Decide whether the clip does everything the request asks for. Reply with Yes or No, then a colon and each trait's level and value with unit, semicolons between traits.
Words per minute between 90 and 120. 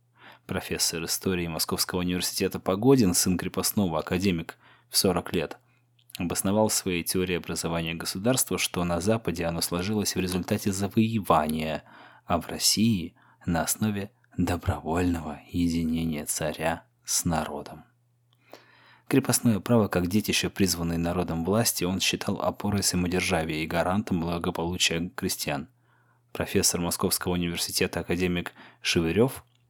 Yes: slow, 110 wpm